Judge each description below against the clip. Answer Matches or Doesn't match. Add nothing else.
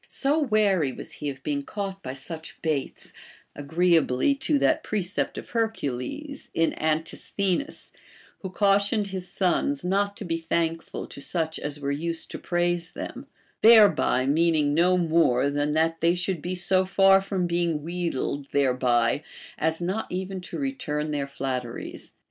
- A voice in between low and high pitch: Matches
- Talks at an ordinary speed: Matches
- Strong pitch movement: Doesn't match